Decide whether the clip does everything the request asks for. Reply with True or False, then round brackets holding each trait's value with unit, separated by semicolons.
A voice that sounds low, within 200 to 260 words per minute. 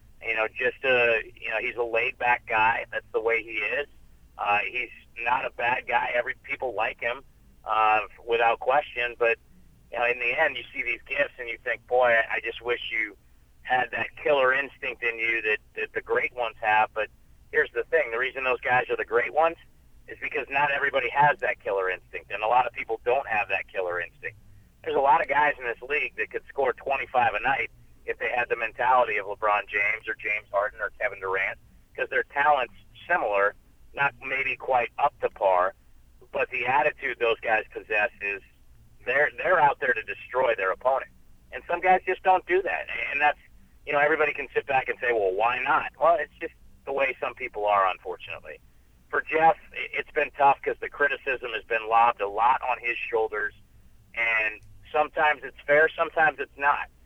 True (120 Hz; 205 wpm)